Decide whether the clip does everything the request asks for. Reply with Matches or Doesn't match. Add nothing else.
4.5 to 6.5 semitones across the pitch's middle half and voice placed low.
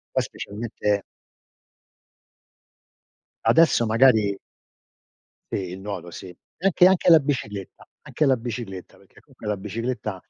Matches